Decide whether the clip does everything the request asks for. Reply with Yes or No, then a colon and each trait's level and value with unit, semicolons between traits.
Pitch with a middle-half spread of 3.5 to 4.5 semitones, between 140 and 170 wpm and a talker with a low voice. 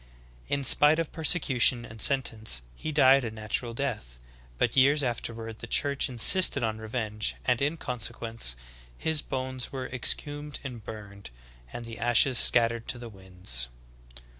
Yes: average, 4.0 semitones; average, 145 wpm; low, 120 Hz